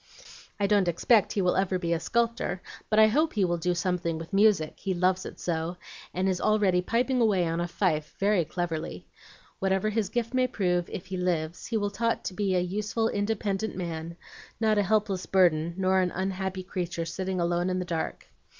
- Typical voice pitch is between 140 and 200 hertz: Yes, medium, 185 Hz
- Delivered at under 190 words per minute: No, fast, 205 wpm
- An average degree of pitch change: Yes, average, 3.1 semitones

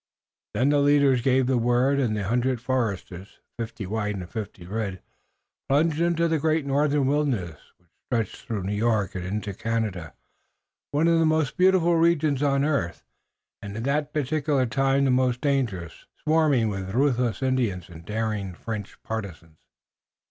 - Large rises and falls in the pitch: Yes, wide, 5.7 semitones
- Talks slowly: No, average, 155 wpm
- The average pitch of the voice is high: No, low, 125 Hz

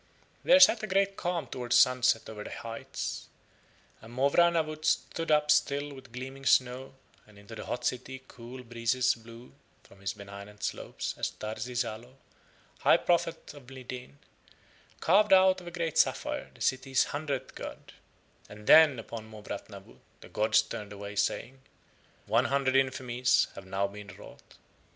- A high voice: No, low, 125 Hz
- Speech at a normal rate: Yes, average, 155 wpm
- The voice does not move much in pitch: No, average, 4.6 semitones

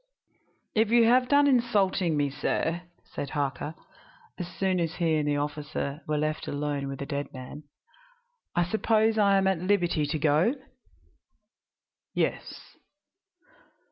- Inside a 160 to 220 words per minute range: No, average, 140 wpm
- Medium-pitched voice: Yes, medium, 165 Hz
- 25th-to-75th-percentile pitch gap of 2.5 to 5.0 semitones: No, wide, 5.5 semitones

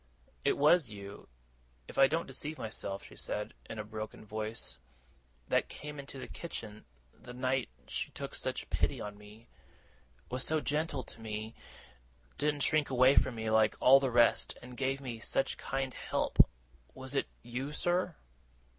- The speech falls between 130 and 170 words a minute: Yes, average, 165 wpm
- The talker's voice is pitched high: No, low, 125 Hz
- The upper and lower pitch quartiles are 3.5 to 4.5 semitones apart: Yes, average, 4.2 semitones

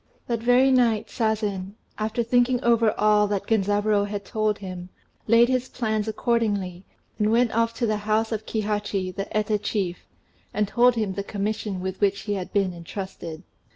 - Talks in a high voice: Yes, high, 210 Hz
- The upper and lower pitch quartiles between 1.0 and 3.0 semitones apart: Yes, narrow, 2.4 semitones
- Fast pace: No, average, 170 wpm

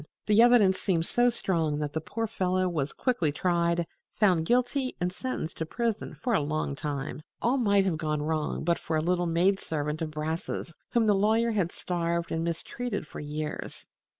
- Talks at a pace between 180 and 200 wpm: Yes, average, 185 wpm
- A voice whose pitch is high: No, medium, 175 Hz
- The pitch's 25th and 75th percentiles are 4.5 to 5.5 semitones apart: Yes, average, 5.2 semitones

